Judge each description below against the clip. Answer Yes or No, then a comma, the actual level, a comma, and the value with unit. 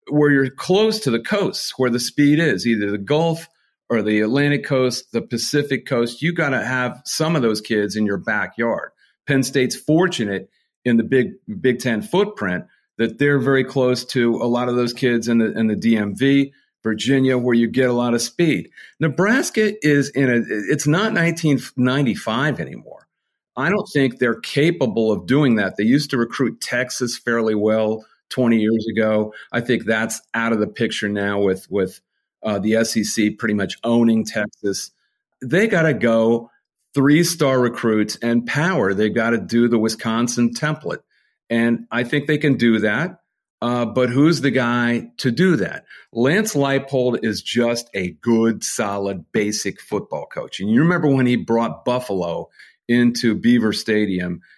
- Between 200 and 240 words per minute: No, average, 175 wpm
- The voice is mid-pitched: No, low, 120 Hz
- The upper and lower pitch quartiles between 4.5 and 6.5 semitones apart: No, average, 3.6 semitones